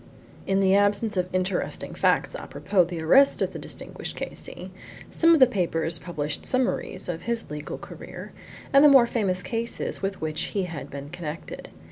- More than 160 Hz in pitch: Yes, high, 190 Hz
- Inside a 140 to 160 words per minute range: No, average, 175 wpm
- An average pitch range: No, wide, 5.8 semitones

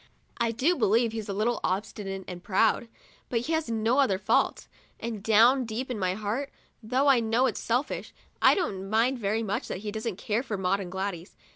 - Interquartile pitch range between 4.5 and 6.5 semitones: No, average, 3.5 semitones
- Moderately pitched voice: No, high, 220 Hz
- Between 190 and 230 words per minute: Yes, average, 200 wpm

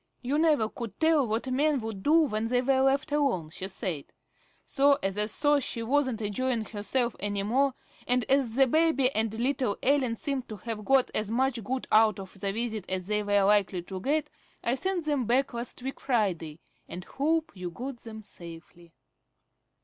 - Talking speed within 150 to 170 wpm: No, average, 190 wpm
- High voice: Yes, high, 235 Hz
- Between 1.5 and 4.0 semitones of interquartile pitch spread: No, average, 4.9 semitones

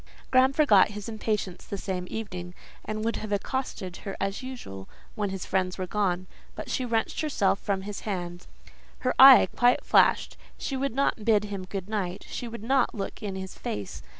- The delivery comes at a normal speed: Yes, average, 185 wpm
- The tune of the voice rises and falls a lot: No, average, 3.7 semitones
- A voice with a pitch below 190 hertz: No, high, 205 Hz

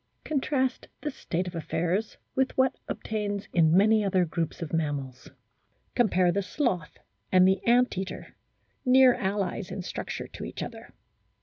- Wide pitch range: Yes, wide, 5.7 semitones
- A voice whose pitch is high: Yes, high, 195 Hz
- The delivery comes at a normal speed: Yes, average, 145 wpm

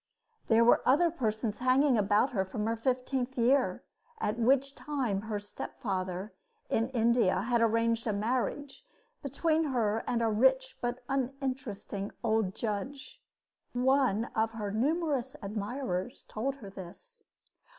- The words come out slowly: Yes, slow, 130 wpm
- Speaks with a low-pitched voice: No, high, 235 Hz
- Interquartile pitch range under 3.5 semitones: No, average, 3.8 semitones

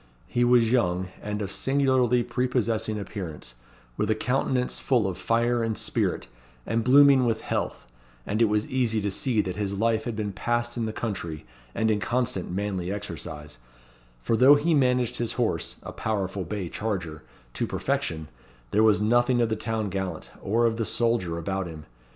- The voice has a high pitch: No, low, 110 Hz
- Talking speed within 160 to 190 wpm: Yes, average, 175 wpm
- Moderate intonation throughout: Yes, average, 3.7 semitones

